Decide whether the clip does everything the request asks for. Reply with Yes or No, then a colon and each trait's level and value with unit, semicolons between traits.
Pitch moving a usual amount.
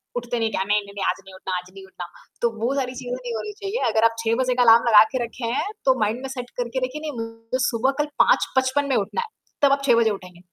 Yes: average, 3.0 semitones